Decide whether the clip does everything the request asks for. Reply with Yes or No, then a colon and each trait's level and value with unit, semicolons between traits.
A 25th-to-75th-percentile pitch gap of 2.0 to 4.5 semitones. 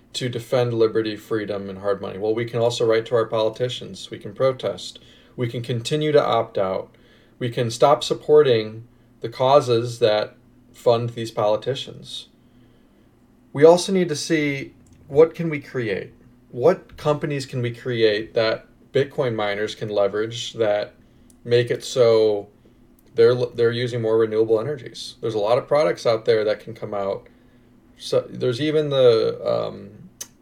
Yes: average, 3.1 semitones